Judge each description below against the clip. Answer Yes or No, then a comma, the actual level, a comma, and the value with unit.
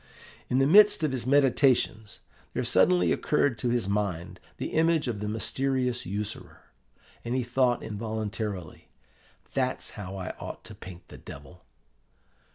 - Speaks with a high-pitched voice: No, low, 115 Hz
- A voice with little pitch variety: No, average, 4.8 semitones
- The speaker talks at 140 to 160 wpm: Yes, average, 145 wpm